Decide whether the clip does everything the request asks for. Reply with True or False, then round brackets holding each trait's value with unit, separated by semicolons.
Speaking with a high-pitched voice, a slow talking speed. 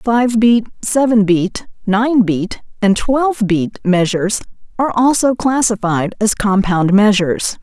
True (215 Hz; 125 wpm)